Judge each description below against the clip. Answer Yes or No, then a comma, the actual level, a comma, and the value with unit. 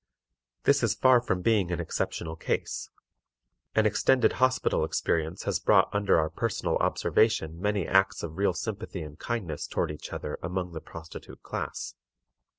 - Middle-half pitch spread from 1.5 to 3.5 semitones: No, average, 5.0 semitones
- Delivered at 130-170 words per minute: Yes, average, 155 wpm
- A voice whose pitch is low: Yes, very low, 90 Hz